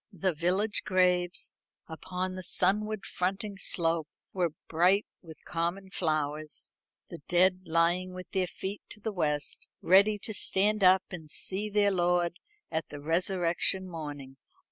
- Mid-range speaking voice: Yes, medium, 180 Hz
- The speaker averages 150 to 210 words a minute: No, average, 140 wpm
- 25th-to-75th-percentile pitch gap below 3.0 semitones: Yes, narrow, 2.6 semitones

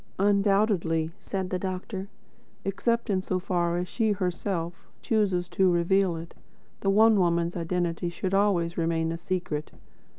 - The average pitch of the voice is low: No, medium, 185 Hz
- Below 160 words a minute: Yes, average, 140 wpm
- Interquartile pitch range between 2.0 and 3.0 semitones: Yes, narrow, 2.4 semitones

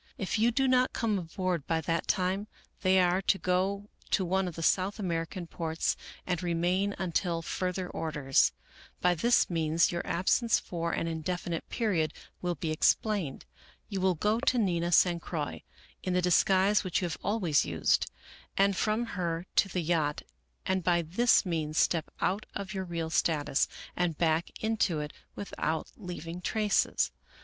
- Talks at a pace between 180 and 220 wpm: No, average, 165 wpm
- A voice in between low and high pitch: Yes, medium, 180 Hz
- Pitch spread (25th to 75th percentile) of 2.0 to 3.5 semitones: Yes, average, 2.9 semitones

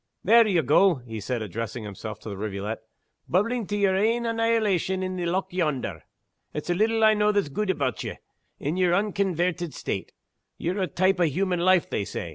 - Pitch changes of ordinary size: No, wide, 6.9 semitones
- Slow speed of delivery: No, average, 190 wpm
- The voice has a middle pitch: Yes, medium, 180 Hz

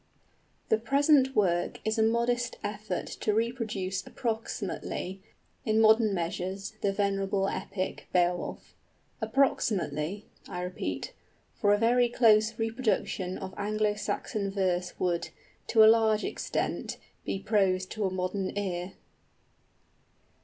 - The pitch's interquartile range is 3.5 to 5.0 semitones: No, average, 3.0 semitones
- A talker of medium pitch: No, high, 205 Hz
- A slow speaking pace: Yes, slow, 115 wpm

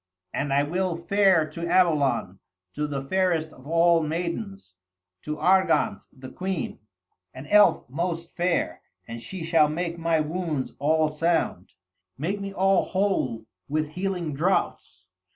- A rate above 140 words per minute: No, slow, 135 wpm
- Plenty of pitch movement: No, average, 3.7 semitones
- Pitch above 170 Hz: No, medium, 165 Hz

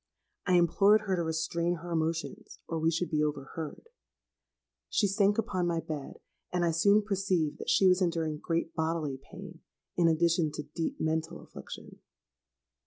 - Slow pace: No, average, 160 wpm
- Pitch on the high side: No, medium, 165 Hz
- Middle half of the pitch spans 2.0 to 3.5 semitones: Yes, narrow, 2.4 semitones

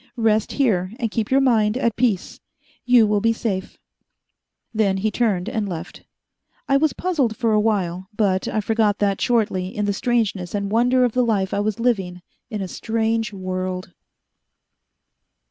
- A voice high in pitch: Yes, high, 215 Hz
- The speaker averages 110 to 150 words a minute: No, average, 165 wpm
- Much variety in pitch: No, average, 3.3 semitones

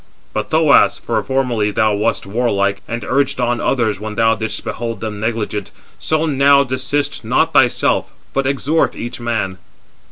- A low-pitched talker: Yes, low, 115 Hz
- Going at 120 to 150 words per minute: Yes, average, 140 wpm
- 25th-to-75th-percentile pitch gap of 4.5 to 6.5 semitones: No, average, 3.8 semitones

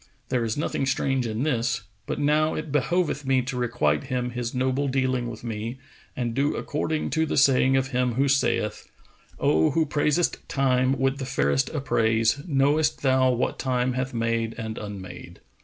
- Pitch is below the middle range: Yes, low, 130 Hz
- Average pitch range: Yes, average, 3.0 semitones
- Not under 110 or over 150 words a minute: No, average, 175 wpm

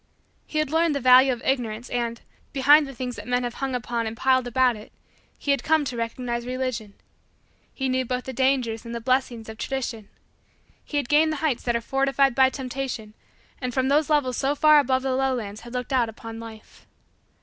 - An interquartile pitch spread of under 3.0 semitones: Yes, narrow, 2.5 semitones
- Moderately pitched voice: No, very high, 255 Hz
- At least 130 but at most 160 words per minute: No, fast, 205 wpm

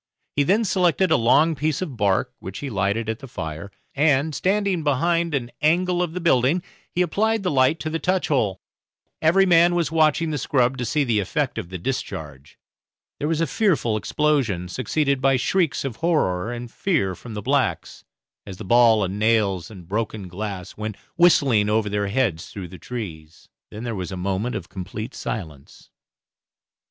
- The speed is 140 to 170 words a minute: No, average, 185 wpm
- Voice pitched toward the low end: Yes, low, 125 Hz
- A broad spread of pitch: Yes, wide, 7.9 semitones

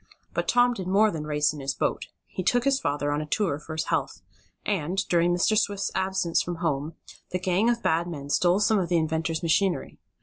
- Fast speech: Yes, fast, 215 wpm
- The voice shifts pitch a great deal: No, average, 4.1 semitones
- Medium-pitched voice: Yes, medium, 175 Hz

